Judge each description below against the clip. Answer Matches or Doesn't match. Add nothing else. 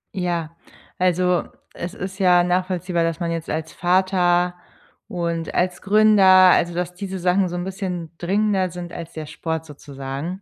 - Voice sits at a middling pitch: Matches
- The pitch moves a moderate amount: Doesn't match